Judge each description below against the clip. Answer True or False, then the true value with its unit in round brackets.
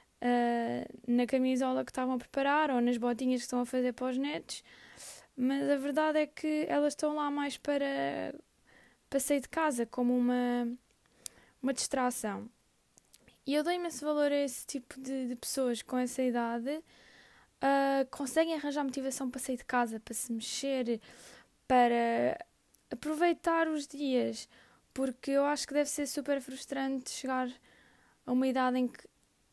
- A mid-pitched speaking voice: False (265 Hz)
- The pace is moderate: True (160 wpm)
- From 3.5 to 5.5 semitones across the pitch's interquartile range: False (2.6 semitones)